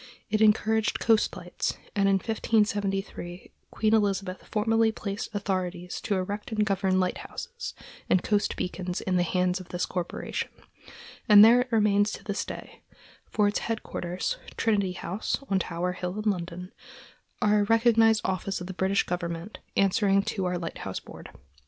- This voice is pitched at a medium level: No, high, 200 Hz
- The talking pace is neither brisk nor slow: Yes, average, 155 wpm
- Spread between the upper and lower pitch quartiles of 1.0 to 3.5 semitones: Yes, average, 2.8 semitones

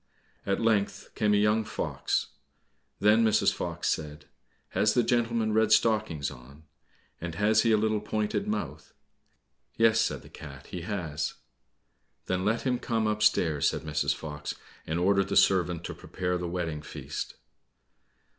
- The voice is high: No, low, 100 Hz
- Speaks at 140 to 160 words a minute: Yes, average, 150 wpm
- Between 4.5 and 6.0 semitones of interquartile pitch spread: Yes, average, 4.9 semitones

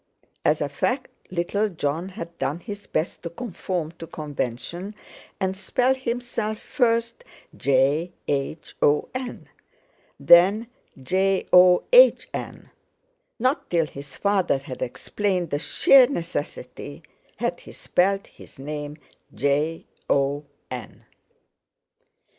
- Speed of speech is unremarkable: No, slow, 95 wpm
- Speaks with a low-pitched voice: No, medium, 175 Hz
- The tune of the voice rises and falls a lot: Yes, wide, 6.4 semitones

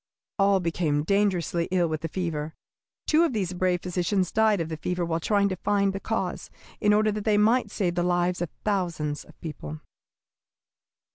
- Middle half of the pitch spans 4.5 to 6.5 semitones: No, average, 3.3 semitones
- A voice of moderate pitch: Yes, medium, 180 Hz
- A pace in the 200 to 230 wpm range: No, average, 185 wpm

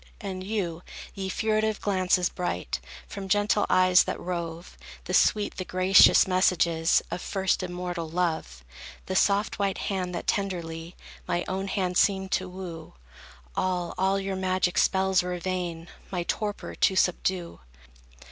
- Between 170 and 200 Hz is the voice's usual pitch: Yes, medium, 185 Hz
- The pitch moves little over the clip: Yes, narrow, 1.6 semitones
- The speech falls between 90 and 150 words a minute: Yes, average, 140 wpm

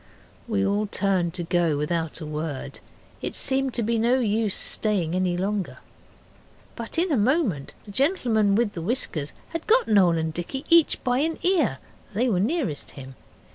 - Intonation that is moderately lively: No, wide, 6.9 semitones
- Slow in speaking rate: No, average, 175 wpm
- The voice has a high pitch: Yes, high, 205 Hz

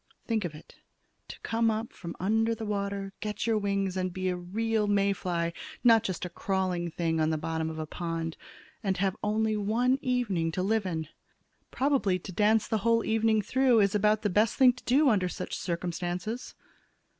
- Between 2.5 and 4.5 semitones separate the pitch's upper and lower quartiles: Yes, average, 3.9 semitones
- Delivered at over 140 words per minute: Yes, average, 190 wpm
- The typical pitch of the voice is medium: No, high, 200 Hz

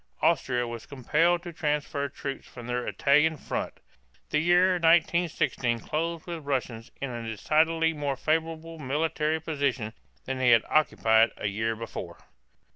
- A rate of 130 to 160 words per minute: Yes, average, 145 wpm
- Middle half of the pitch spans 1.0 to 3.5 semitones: No, average, 4.9 semitones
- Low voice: No, medium, 145 Hz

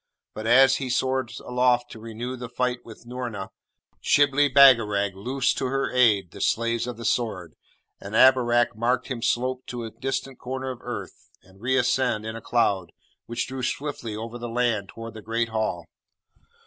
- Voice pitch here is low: Yes, low, 120 Hz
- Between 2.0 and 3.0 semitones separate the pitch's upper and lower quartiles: Yes, narrow, 2.4 semitones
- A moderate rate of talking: Yes, average, 175 wpm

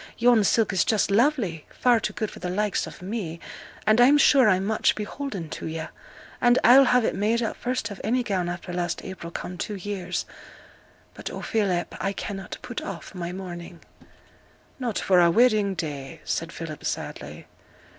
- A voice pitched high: Yes, high, 200 Hz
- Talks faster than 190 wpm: No, average, 180 wpm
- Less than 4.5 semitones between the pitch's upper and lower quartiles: No, average, 4.8 semitones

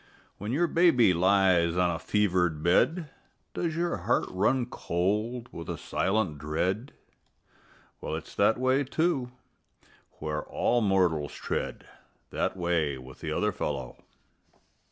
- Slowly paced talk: Yes, slow, 130 wpm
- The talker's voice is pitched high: No, very low, 95 Hz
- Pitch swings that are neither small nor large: No, wide, 6.9 semitones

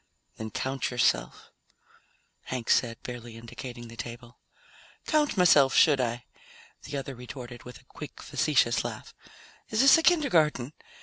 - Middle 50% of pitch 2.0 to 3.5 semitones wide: No, average, 4.0 semitones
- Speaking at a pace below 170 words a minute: Yes, slow, 135 wpm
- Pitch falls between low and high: No, low, 125 Hz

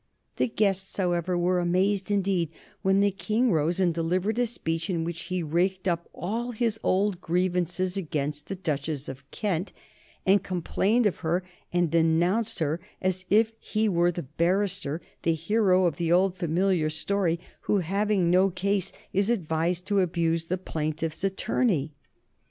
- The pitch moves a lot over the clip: No, average, 3.0 semitones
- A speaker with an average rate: Yes, average, 155 wpm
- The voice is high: No, medium, 180 Hz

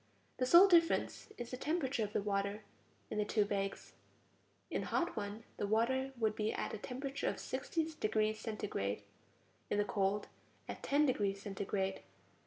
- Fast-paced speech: No, average, 170 wpm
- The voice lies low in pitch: No, high, 215 Hz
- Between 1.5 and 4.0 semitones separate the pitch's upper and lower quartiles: No, average, 4.5 semitones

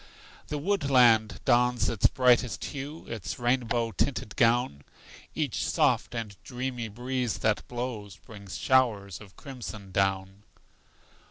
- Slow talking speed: Yes, slow, 115 wpm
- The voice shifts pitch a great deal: No, average, 3.6 semitones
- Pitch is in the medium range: No, low, 120 Hz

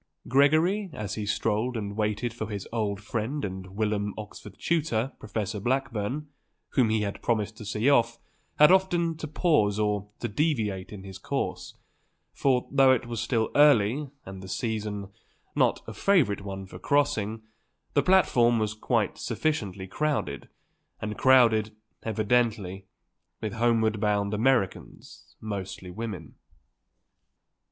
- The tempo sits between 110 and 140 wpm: Yes, slow, 135 wpm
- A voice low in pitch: Yes, low, 110 Hz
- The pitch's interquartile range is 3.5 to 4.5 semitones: Yes, average, 4.2 semitones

